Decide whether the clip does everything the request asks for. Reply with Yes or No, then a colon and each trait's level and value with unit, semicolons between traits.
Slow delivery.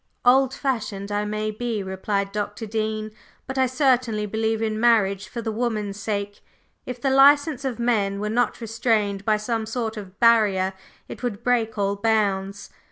No: average, 165 wpm